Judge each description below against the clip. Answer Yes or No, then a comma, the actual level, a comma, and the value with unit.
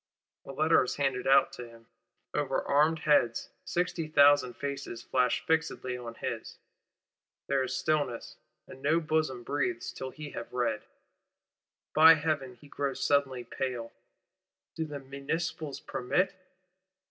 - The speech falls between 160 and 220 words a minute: No, slow, 135 wpm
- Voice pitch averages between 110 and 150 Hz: Yes, medium, 140 Hz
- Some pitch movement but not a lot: Yes, average, 3.4 semitones